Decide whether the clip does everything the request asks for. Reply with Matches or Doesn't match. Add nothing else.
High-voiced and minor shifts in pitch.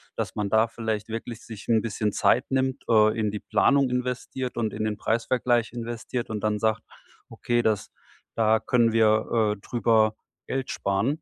Doesn't match